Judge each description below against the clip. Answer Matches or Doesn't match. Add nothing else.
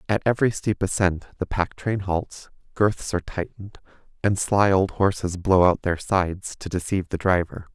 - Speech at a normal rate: Matches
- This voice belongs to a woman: Doesn't match